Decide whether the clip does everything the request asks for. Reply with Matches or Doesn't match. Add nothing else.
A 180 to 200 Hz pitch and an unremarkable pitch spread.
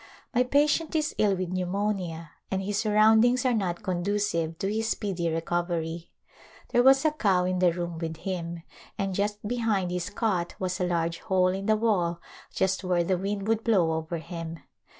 Matches